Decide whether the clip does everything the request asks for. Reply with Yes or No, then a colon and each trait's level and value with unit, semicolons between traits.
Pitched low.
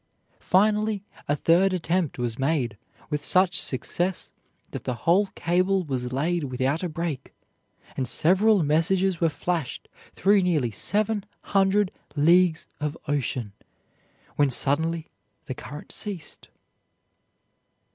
No: medium, 165 Hz